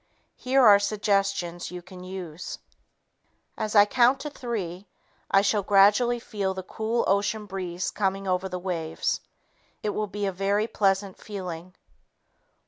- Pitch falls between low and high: No, high, 195 Hz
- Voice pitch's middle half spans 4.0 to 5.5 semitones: No, narrow, 2.4 semitones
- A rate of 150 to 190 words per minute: No, average, 140 wpm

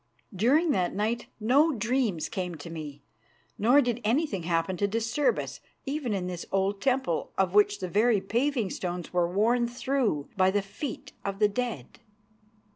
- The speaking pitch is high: Yes, high, 210 Hz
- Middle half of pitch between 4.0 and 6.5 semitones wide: Yes, average, 4.9 semitones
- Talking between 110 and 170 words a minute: Yes, average, 165 wpm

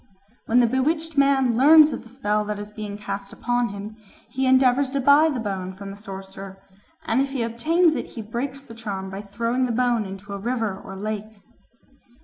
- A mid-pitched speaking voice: No, high, 230 Hz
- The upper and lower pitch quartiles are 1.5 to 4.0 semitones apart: No, average, 4.6 semitones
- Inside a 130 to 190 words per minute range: No, average, 200 wpm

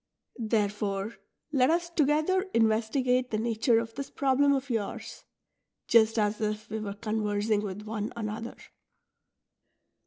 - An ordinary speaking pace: No, slow, 125 wpm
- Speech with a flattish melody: No, average, 3.5 semitones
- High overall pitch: Yes, high, 225 Hz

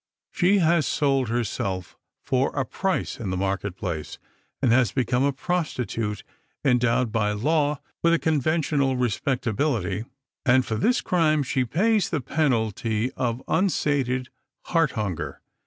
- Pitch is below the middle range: Yes, low, 130 Hz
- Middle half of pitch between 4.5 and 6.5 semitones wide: Yes, wide, 5.4 semitones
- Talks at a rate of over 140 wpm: No, slow, 135 wpm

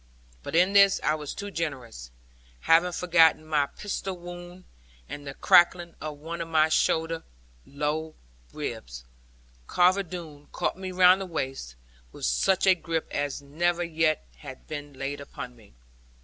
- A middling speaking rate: Yes, average, 150 wpm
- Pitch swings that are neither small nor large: Yes, average, 3.5 semitones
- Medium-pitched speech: Yes, medium, 160 Hz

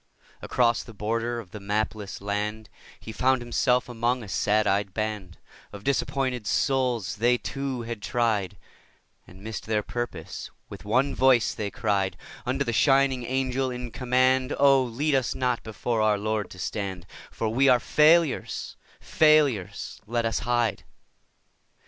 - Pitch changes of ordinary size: Yes, average, 3.4 semitones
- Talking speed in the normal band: Yes, average, 150 wpm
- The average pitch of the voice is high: No, low, 120 Hz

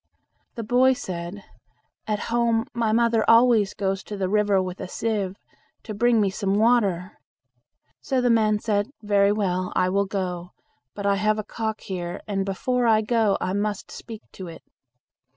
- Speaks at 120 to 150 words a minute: No, average, 170 wpm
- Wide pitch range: No, average, 2.8 semitones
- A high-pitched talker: Yes, high, 210 Hz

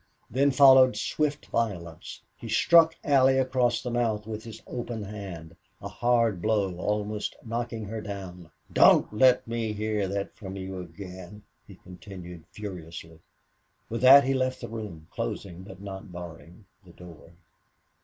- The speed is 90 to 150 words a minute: Yes, average, 145 wpm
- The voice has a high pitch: No, low, 105 Hz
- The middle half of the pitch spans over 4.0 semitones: Yes, average, 4.6 semitones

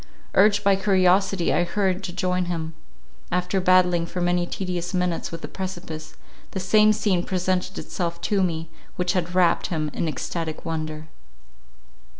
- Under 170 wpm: Yes, average, 150 wpm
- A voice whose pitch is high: No, medium, 180 Hz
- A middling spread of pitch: No, narrow, 1.9 semitones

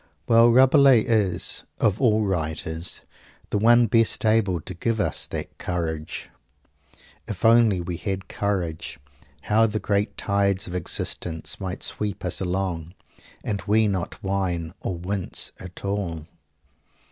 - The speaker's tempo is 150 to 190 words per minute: No, slow, 135 wpm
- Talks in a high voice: No, low, 100 Hz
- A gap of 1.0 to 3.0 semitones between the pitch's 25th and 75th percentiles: No, average, 3.7 semitones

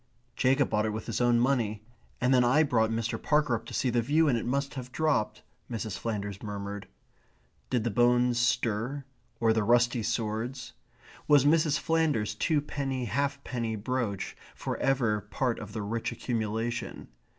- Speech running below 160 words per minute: No, average, 165 wpm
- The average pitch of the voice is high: No, low, 120 Hz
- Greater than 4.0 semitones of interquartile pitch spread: No, average, 3.4 semitones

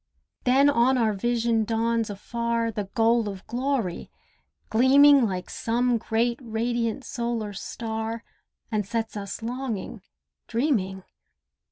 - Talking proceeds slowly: Yes, slow, 115 wpm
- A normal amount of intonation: No, narrow, 1.7 semitones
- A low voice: No, high, 230 Hz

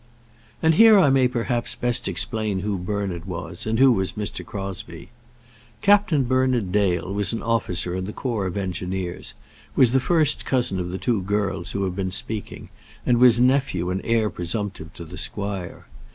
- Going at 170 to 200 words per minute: Yes, average, 175 wpm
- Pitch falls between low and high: No, low, 105 Hz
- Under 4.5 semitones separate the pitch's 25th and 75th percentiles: No, average, 4.8 semitones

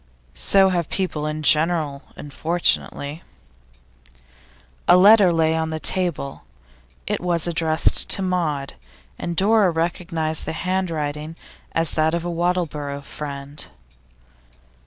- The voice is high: No, medium, 165 Hz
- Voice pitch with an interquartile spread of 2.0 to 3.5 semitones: Yes, average, 2.8 semitones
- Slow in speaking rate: Yes, slow, 115 wpm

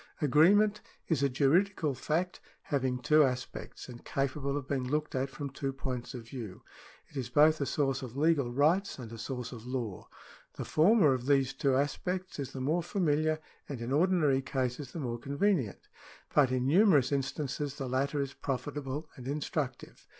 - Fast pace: No, average, 175 wpm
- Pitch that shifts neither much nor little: Yes, average, 3.0 semitones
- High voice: No, medium, 140 Hz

